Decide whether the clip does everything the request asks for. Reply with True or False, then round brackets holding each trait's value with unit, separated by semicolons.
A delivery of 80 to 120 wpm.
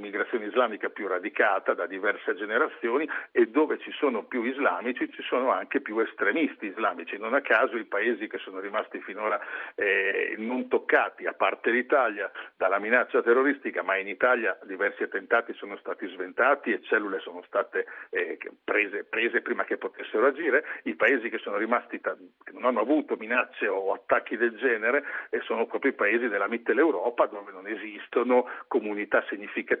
False (165 wpm)